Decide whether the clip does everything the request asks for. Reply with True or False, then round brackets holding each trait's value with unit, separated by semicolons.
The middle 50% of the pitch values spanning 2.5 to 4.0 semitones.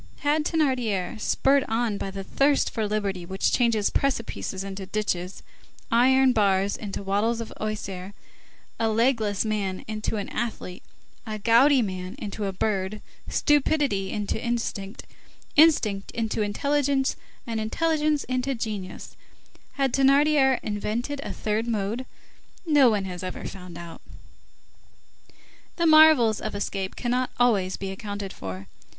False (5.0 semitones)